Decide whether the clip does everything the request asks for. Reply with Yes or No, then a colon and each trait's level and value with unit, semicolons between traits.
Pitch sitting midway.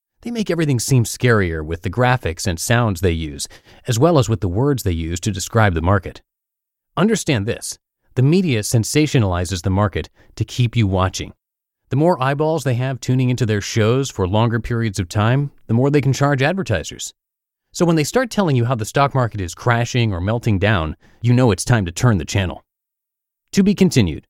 No: low, 120 Hz